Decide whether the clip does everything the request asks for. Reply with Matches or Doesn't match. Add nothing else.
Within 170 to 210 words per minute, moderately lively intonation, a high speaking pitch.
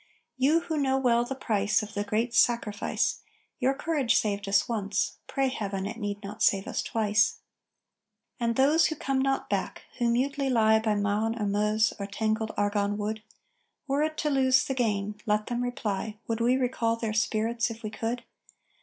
Matches